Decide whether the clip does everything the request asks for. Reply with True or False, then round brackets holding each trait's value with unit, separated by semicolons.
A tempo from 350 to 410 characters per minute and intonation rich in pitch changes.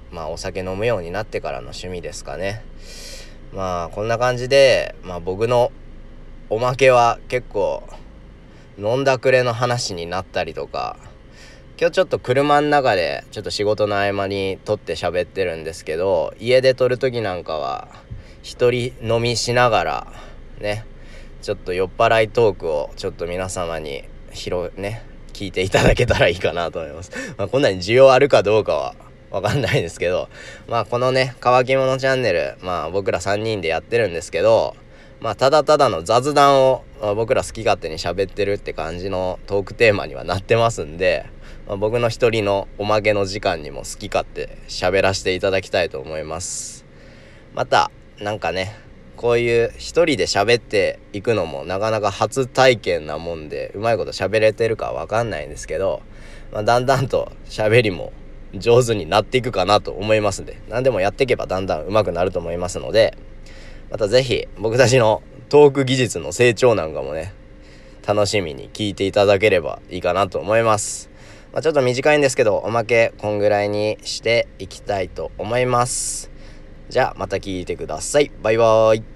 False (355 characters per minute; 4.5 semitones)